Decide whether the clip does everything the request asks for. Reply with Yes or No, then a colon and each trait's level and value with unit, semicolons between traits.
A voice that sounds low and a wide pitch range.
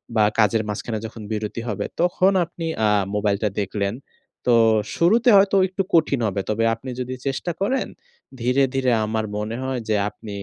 Yes: low, 115 Hz; wide, 7.7 semitones